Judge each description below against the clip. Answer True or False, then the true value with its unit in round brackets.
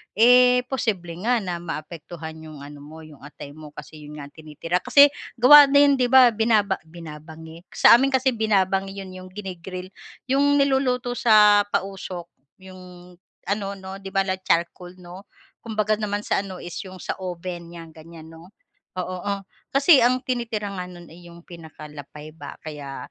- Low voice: False (185 Hz)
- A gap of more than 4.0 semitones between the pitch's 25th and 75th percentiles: True (5.1 semitones)